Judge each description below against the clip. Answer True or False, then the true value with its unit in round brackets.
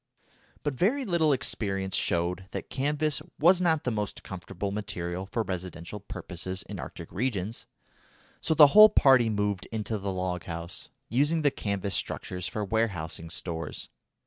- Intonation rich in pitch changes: True (7.2 semitones)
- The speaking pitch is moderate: False (105 Hz)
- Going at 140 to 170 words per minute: True (145 wpm)